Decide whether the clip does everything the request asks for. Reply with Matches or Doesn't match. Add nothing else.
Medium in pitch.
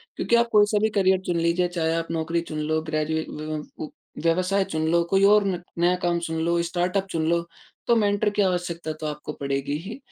Matches